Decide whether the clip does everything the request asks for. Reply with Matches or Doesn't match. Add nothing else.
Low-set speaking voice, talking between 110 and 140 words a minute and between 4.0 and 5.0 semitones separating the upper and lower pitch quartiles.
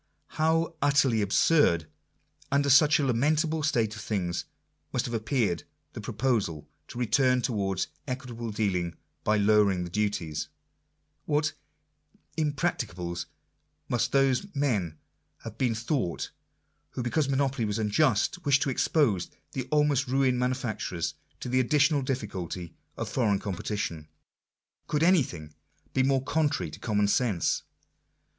Doesn't match